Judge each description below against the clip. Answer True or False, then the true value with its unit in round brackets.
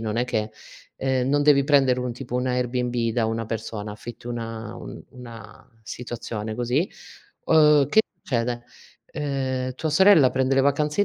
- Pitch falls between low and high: False (125 Hz)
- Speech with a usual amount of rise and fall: True (3.1 semitones)